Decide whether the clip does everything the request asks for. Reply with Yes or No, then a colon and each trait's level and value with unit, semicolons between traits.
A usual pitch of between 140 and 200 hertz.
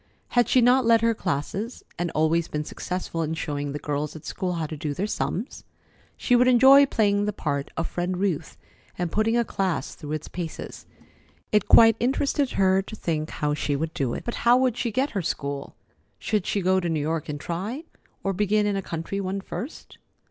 Yes: medium, 185 Hz